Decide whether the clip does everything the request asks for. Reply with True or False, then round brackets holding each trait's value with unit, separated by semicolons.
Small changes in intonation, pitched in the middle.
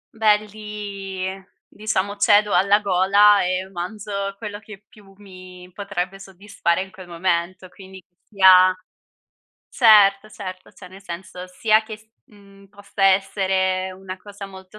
False (1.7 semitones; 195 Hz)